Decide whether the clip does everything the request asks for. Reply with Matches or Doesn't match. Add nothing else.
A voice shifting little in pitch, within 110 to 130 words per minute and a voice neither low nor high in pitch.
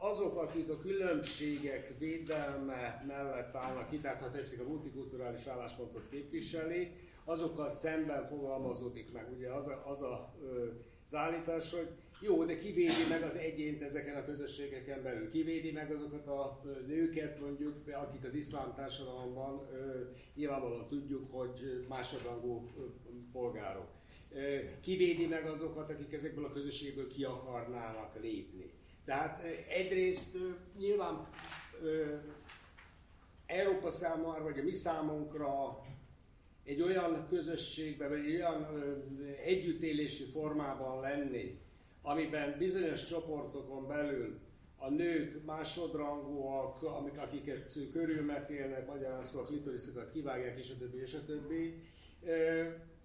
Doesn't match